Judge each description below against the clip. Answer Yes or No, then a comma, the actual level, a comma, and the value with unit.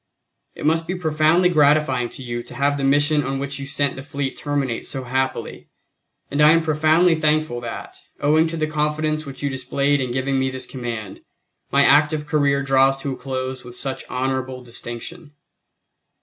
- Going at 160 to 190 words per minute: Yes, average, 180 wpm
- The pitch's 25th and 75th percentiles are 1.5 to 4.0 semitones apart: Yes, narrow, 2.6 semitones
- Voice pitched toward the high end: No, medium, 140 Hz